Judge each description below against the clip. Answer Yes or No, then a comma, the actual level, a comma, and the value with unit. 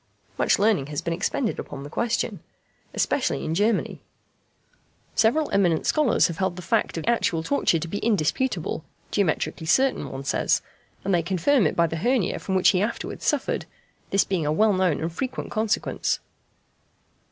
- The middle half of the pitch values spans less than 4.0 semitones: No, wide, 5.5 semitones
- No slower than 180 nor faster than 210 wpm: No, average, 165 wpm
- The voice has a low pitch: No, high, 190 Hz